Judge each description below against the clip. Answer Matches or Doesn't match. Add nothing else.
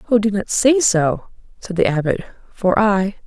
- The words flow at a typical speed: Matches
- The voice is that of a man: Doesn't match